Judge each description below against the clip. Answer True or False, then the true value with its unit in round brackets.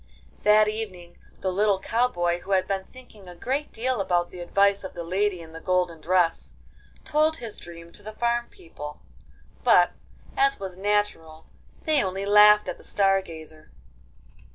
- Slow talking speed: False (170 wpm)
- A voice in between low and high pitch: False (195 Hz)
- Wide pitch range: False (3.5 semitones)